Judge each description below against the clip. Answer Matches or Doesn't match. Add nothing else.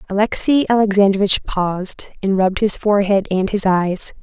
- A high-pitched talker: Matches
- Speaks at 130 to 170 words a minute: Matches